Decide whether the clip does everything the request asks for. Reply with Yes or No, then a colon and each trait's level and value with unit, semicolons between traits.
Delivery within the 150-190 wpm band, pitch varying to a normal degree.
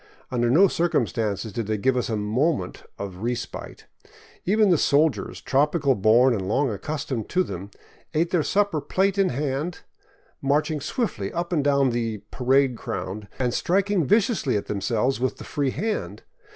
No: average, 170 wpm; wide, 7.0 semitones